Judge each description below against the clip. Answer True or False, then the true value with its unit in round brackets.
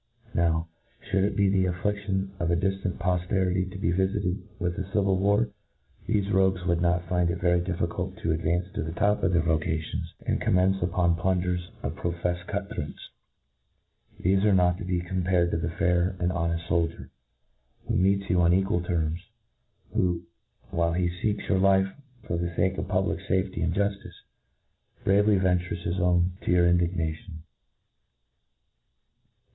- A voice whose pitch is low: True (90 Hz)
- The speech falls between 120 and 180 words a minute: True (165 wpm)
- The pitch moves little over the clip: True (1.9 semitones)